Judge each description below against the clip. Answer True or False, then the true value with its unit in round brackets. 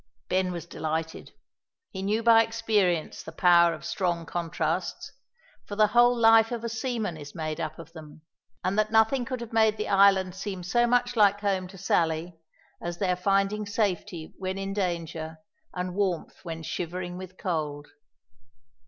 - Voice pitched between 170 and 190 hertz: True (185 Hz)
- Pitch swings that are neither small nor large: True (4.1 semitones)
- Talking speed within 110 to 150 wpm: False (165 wpm)